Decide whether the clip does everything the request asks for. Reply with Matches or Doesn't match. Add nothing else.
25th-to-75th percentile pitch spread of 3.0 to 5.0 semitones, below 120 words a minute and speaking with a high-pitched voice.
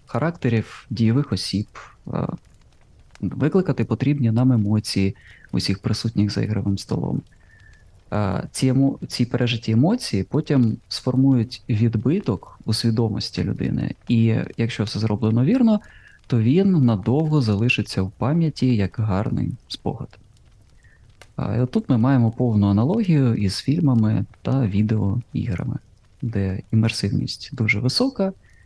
Doesn't match